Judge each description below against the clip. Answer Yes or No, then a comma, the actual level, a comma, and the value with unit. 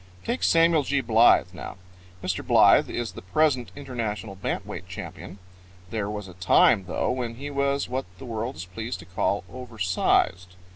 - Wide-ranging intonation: Yes, wide, 6.0 semitones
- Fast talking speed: No, average, 175 wpm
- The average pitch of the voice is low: Yes, low, 115 Hz